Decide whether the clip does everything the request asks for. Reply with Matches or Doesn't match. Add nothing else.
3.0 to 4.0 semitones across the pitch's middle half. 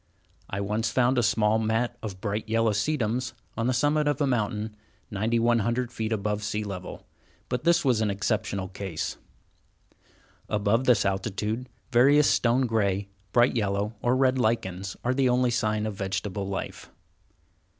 Matches